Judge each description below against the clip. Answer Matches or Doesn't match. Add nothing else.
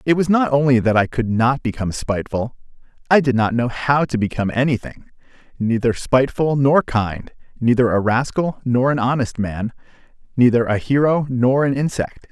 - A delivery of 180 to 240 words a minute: Doesn't match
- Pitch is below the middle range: Matches